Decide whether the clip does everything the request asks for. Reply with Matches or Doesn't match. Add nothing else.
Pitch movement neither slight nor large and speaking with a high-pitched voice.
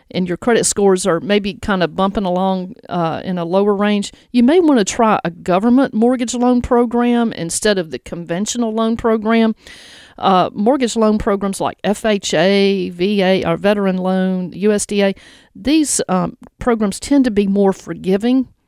Matches